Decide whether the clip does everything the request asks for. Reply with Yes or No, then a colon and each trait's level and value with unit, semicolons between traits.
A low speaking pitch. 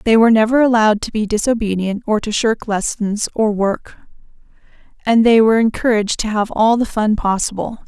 No: high, 220 Hz